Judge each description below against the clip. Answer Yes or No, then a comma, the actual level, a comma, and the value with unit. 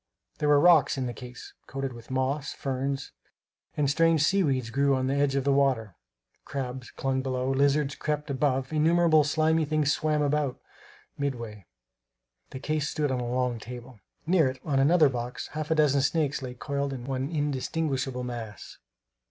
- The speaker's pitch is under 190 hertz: Yes, medium, 140 Hz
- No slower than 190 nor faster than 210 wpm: No, average, 170 wpm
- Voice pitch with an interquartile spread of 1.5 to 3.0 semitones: Yes, average, 2.7 semitones